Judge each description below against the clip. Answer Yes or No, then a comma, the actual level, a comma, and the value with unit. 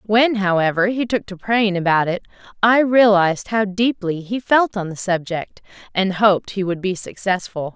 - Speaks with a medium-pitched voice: No, high, 200 Hz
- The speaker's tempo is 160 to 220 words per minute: Yes, average, 180 wpm